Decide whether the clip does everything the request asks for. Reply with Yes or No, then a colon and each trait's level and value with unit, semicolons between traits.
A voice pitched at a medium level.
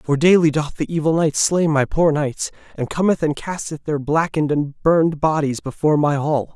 Yes: medium, 155 Hz